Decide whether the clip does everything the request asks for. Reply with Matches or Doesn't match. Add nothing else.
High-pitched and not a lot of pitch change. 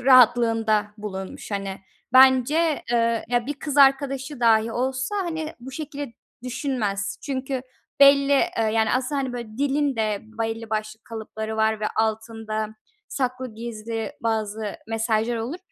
Doesn't match